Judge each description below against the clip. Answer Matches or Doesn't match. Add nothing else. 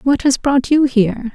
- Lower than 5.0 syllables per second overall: Matches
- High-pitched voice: Matches